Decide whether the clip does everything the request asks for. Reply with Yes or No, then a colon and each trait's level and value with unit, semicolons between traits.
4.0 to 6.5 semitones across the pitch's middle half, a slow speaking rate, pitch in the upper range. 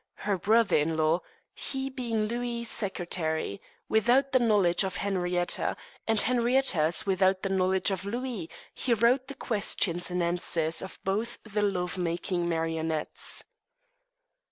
Yes: average, 5.1 semitones; slow, 130 wpm; high, 195 Hz